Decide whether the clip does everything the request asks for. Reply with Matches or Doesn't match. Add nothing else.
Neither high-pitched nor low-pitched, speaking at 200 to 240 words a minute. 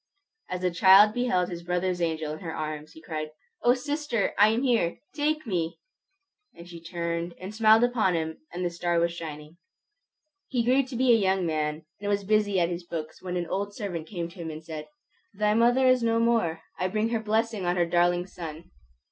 Matches